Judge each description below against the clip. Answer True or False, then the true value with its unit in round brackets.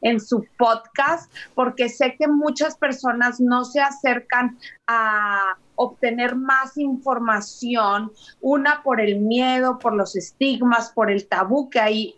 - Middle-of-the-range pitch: False (245 Hz)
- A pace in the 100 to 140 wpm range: True (135 wpm)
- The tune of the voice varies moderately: True (3.4 semitones)